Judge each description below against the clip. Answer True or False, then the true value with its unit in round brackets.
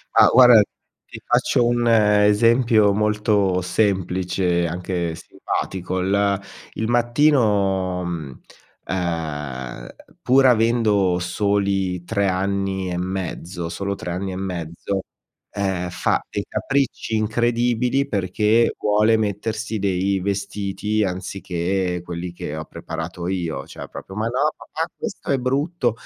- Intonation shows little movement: False (3.6 semitones)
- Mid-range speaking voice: False (100 Hz)